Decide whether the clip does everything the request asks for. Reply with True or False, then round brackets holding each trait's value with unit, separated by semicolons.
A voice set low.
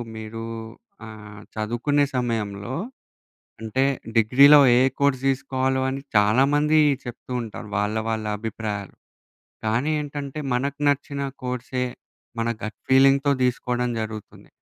True (125 Hz)